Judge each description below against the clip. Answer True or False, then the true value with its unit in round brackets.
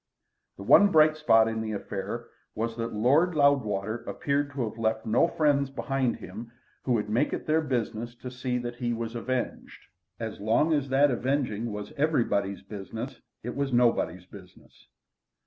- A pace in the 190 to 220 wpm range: False (165 wpm)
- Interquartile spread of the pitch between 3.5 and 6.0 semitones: True (4.1 semitones)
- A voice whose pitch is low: True (120 Hz)